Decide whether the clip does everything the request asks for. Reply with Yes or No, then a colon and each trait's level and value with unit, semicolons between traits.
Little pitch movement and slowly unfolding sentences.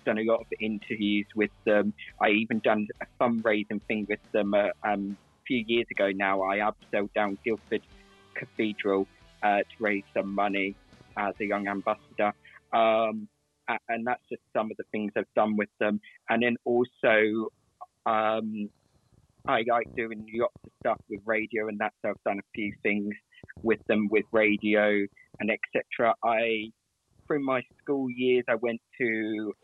No: narrow, 1.6 semitones; average, 165 wpm